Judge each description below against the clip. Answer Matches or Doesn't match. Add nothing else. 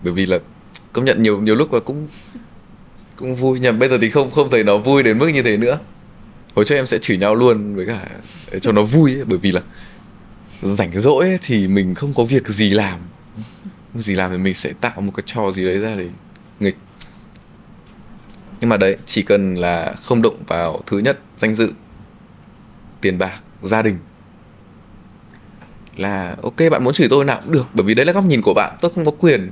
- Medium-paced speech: Matches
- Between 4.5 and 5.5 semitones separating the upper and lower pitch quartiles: Matches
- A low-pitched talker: Matches